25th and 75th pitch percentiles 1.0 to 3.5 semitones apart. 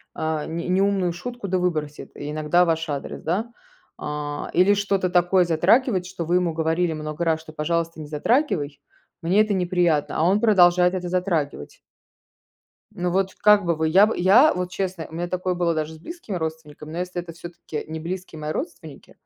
Yes: average, 2.8 semitones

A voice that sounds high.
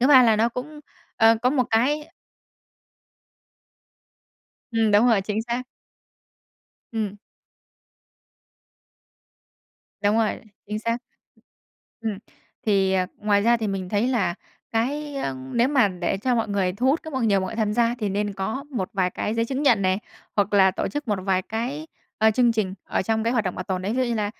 Yes: high, 220 Hz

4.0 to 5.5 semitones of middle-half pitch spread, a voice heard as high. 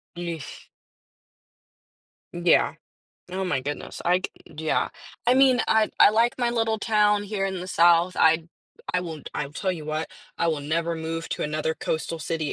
No: average, 4.4 semitones; medium, 170 Hz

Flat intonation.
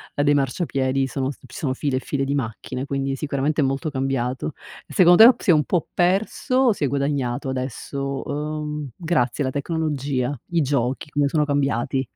Yes: narrow, 2.3 semitones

